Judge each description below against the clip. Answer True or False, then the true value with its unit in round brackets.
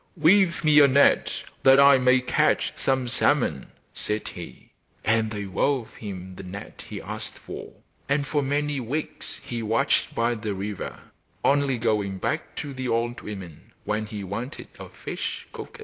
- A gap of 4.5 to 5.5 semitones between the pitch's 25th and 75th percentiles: True (5.0 semitones)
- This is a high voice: False (120 Hz)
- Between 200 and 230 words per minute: False (165 wpm)